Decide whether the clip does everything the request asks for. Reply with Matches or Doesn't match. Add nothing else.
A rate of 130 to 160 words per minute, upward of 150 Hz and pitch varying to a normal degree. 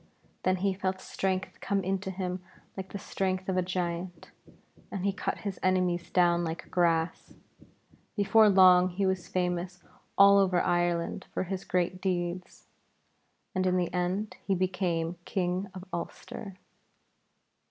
Doesn't match